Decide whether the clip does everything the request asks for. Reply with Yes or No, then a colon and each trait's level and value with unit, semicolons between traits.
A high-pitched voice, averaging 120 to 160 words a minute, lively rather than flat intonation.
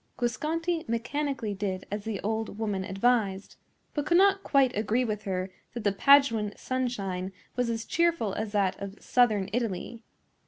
No: high, 225 Hz; average, 155 wpm; average, 4.4 semitones